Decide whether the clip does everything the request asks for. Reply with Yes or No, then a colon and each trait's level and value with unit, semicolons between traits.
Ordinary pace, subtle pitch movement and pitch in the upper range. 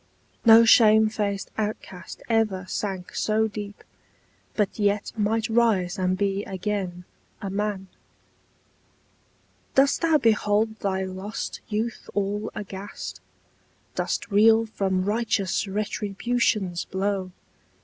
No: slow, 105 wpm; narrow, 2.3 semitones; high, 205 Hz